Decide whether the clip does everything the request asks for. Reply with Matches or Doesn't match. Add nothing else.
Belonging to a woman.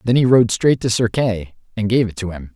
Doesn't match